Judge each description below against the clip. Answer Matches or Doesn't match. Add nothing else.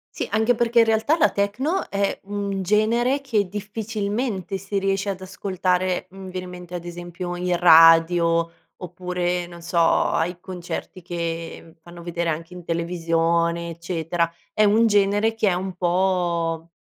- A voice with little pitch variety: Doesn't match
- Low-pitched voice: Doesn't match